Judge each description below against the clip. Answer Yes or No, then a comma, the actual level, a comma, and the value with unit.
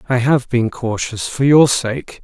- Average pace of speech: Yes, average, 160 wpm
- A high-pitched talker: No, low, 125 Hz